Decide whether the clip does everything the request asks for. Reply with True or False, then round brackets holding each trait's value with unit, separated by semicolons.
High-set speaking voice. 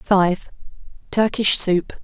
True (195 Hz)